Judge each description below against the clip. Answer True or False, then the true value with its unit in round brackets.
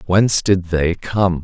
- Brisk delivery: False (165 wpm)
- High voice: False (90 Hz)